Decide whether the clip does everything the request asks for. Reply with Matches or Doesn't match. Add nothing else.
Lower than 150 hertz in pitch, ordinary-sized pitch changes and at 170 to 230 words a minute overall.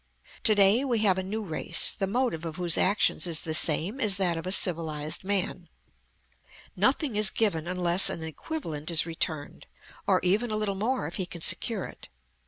Doesn't match